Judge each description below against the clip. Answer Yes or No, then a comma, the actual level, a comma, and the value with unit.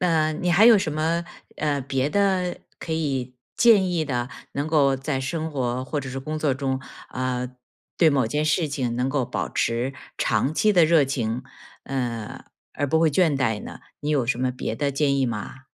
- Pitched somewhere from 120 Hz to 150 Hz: Yes, medium, 140 Hz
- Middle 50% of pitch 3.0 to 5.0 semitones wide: Yes, average, 3.6 semitones